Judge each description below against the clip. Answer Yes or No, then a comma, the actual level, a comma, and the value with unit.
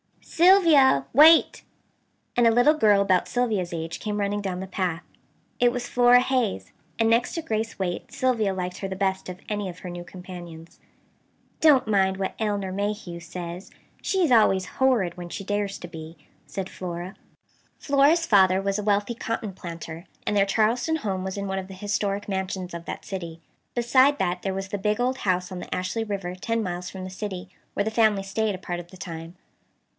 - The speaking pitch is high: Yes, high, 195 Hz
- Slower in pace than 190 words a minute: No, average, 195 wpm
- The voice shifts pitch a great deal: No, average, 3.7 semitones